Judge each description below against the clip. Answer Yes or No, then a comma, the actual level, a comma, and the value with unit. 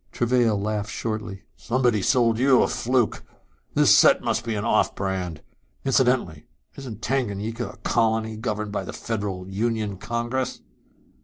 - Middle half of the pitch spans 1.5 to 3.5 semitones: Yes, average, 2.8 semitones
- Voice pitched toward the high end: No, low, 110 Hz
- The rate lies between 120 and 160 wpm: Yes, average, 140 wpm